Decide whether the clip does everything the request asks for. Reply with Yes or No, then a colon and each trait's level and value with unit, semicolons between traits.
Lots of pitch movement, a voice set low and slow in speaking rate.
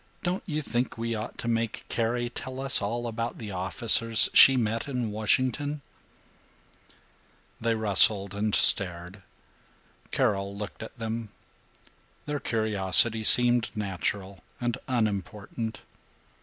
No: average, 2.8 semitones; low, 115 Hz; slow, 115 wpm